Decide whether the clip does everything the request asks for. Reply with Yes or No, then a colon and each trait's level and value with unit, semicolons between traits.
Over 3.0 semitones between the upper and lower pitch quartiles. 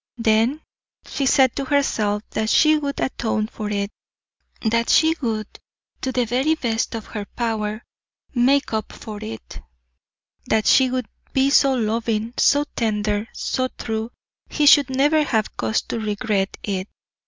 Yes: average, 3.8 semitones